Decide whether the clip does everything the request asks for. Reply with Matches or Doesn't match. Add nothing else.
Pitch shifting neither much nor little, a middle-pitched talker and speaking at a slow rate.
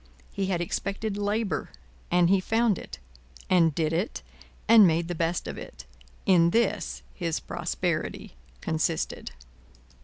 Matches